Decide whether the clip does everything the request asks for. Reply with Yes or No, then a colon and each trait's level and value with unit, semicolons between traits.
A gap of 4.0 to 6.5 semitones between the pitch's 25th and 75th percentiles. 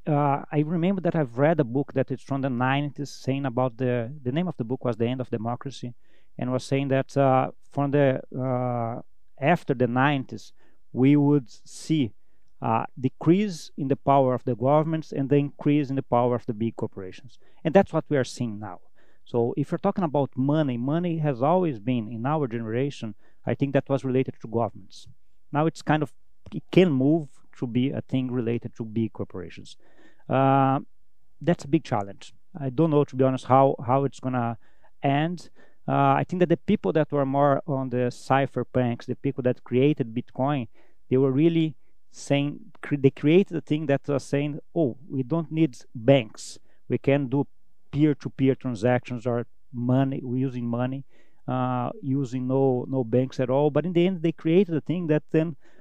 No: average, 2.9 semitones